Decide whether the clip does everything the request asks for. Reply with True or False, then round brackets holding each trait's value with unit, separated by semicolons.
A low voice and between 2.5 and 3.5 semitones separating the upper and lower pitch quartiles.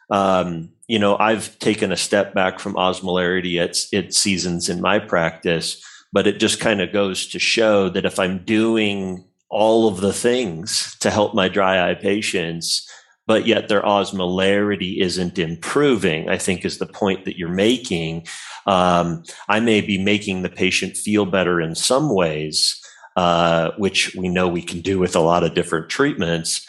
True (95 Hz; 2.8 semitones)